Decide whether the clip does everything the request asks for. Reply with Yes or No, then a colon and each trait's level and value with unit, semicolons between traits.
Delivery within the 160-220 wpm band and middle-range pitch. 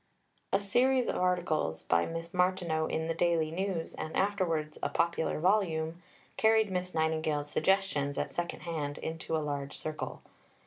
No: average, 150 wpm; medium, 165 Hz